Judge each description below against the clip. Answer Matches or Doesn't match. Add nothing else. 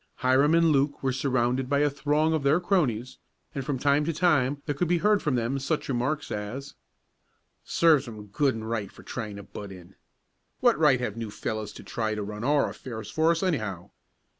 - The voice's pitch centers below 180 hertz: Matches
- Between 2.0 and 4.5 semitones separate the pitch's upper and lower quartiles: Doesn't match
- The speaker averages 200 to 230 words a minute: Matches